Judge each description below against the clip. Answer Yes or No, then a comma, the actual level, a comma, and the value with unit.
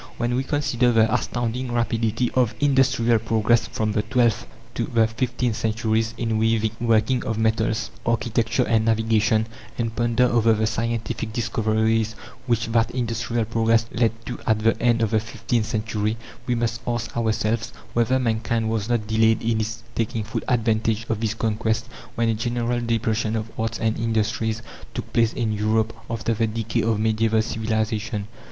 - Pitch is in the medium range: No, low, 115 Hz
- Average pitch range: No, narrow, 1.1 semitones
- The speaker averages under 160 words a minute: No, average, 165 wpm